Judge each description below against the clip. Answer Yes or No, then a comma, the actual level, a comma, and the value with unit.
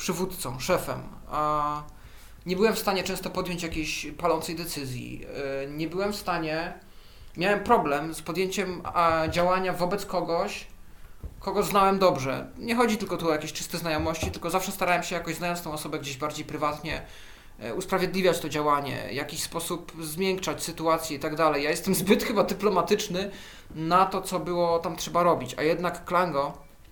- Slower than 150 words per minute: No, fast, 160 wpm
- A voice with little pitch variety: No, average, 3.6 semitones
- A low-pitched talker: No, medium, 170 Hz